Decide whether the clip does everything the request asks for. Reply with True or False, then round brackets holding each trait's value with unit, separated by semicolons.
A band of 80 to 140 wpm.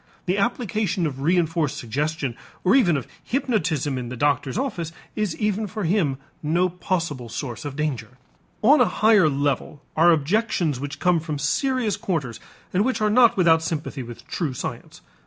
False (165 wpm)